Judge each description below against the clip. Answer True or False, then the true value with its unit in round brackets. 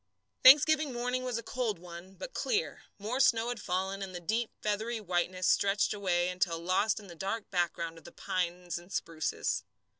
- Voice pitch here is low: False (195 Hz)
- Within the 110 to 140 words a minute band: False (180 wpm)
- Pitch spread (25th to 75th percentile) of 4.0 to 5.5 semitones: True (4.9 semitones)